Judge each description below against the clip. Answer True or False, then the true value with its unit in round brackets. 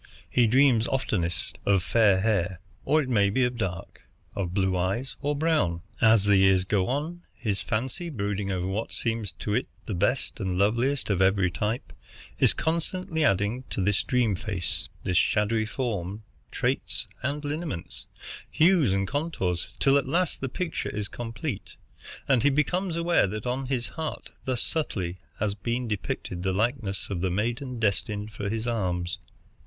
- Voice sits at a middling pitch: False (110 Hz)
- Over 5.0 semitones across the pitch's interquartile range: True (5.5 semitones)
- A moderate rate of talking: True (165 wpm)